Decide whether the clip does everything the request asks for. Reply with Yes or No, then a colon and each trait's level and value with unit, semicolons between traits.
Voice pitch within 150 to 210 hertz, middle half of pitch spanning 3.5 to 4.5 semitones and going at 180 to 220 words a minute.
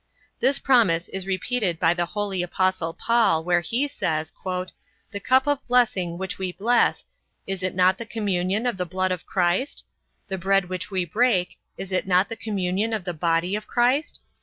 Yes: high, 190 Hz; average, 3.9 semitones; average, 185 wpm